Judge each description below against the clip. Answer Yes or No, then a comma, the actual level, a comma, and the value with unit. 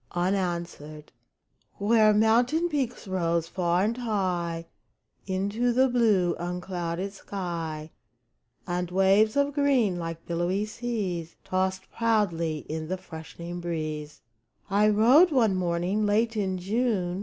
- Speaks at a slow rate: Yes, slow, 115 wpm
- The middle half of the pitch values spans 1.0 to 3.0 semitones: No, average, 4.2 semitones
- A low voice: No, high, 190 Hz